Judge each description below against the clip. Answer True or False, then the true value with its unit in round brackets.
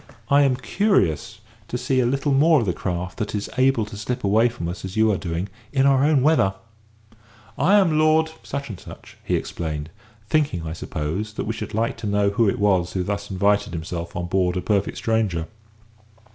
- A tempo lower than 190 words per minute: False (200 wpm)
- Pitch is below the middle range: True (105 Hz)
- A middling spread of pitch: False (6.5 semitones)